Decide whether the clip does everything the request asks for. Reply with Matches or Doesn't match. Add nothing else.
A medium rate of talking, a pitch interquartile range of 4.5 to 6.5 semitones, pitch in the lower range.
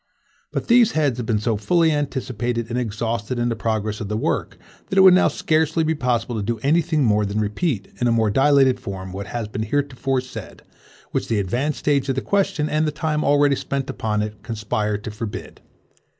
Doesn't match